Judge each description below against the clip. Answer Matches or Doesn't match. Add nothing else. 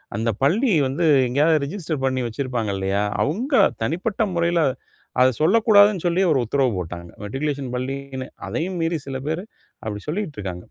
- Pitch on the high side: Doesn't match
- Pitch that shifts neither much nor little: Doesn't match